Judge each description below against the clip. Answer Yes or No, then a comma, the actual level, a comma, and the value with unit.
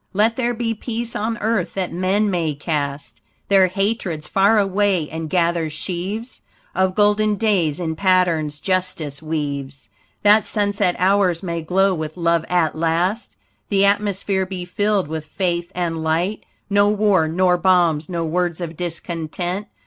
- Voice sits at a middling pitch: Yes, medium, 180 Hz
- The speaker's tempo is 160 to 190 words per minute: No, average, 150 wpm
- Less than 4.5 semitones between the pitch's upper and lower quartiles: Yes, average, 3.7 semitones